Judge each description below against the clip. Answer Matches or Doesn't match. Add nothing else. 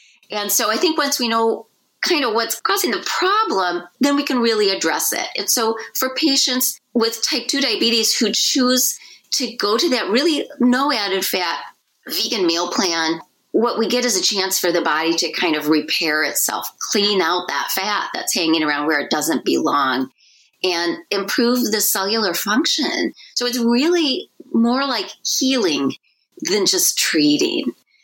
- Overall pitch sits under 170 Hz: Doesn't match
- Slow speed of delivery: Doesn't match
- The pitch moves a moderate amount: Doesn't match